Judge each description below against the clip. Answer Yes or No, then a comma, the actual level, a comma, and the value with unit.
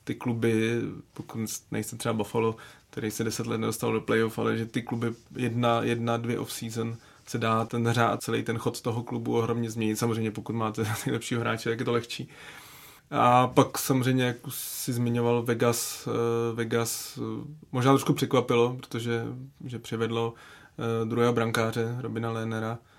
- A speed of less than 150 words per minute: No, average, 155 wpm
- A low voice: Yes, low, 115 Hz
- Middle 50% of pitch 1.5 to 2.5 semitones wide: Yes, narrow, 1.8 semitones